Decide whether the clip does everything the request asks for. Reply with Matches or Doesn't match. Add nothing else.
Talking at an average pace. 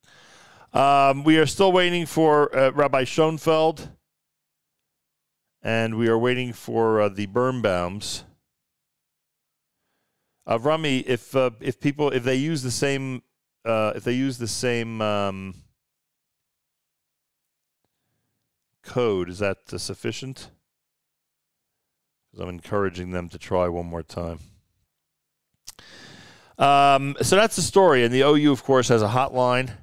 Doesn't match